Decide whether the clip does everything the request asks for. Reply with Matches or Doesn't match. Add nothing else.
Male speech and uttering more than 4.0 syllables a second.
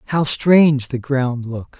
Doesn't match